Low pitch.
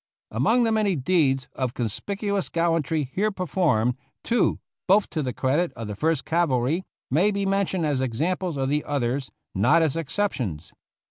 No: medium, 155 Hz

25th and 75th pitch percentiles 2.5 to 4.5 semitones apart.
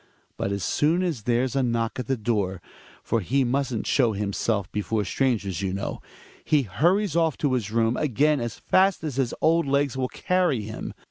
No: average, 5.2 semitones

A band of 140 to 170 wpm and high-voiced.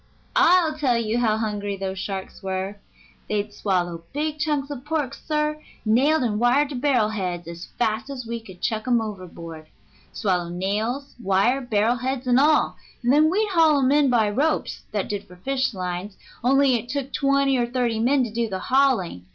No: average, 185 wpm; high, 235 Hz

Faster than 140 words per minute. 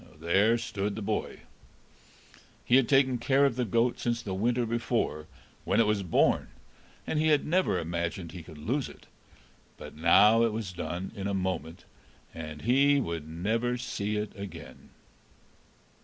Yes: average, 160 wpm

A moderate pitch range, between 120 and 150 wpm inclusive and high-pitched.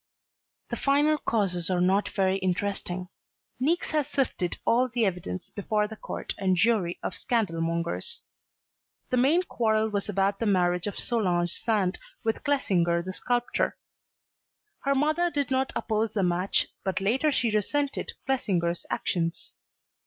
No: wide, 5.9 semitones; average, 145 wpm; high, 210 Hz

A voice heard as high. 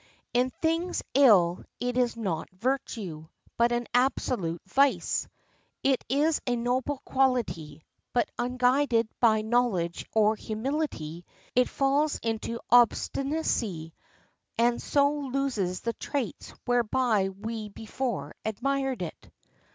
Yes: high, 240 Hz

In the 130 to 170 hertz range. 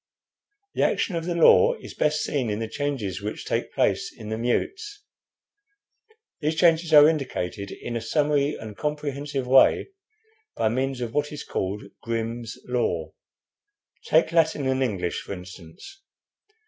Yes: low, 135 Hz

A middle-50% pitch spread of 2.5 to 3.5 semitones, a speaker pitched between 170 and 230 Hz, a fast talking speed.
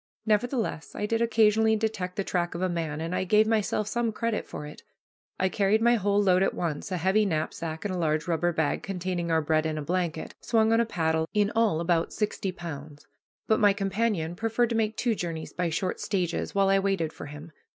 No: average, 4.7 semitones; medium, 185 Hz; fast, 215 wpm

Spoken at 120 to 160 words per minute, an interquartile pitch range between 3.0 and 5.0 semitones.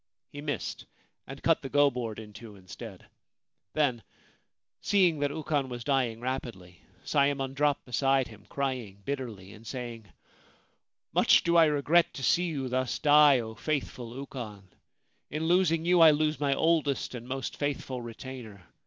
Yes: average, 155 wpm; average, 4.0 semitones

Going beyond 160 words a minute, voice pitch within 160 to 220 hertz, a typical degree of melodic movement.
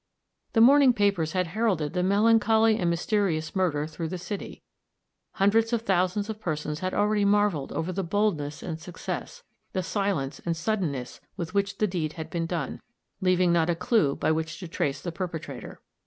Yes: average, 175 wpm; medium, 185 Hz; average, 4.3 semitones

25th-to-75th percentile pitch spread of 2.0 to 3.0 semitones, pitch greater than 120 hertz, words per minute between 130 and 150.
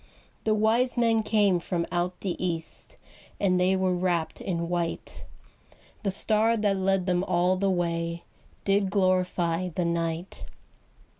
Yes: narrow, 2.4 semitones; medium, 185 Hz; average, 140 wpm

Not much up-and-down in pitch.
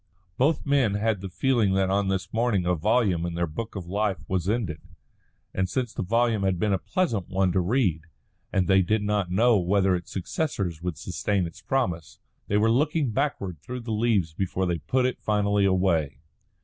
No: average, 4.0 semitones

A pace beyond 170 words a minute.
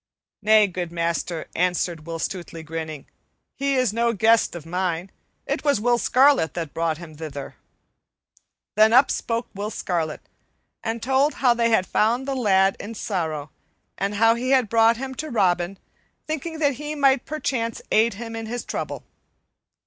No: average, 165 wpm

